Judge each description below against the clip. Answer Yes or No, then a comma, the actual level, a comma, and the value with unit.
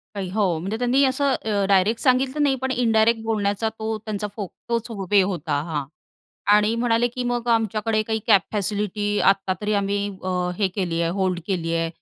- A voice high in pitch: Yes, high, 210 Hz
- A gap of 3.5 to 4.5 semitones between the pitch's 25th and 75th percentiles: No, average, 2.9 semitones